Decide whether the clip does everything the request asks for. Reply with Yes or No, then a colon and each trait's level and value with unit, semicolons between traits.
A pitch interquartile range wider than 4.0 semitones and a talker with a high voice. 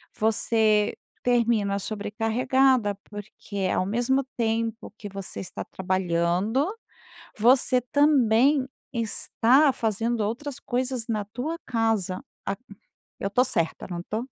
No: average, 3.5 semitones; high, 225 Hz